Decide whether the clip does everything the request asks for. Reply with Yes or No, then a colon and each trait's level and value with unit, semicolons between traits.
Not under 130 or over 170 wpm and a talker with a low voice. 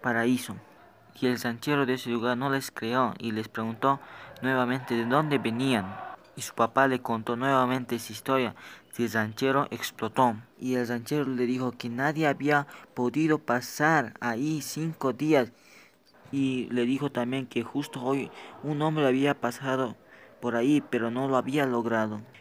Yes: average, 160 wpm; low, 130 Hz